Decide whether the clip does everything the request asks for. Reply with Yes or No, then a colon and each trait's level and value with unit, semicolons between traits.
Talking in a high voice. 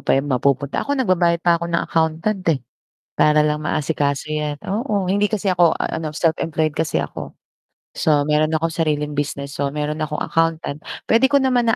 No: medium, 160 Hz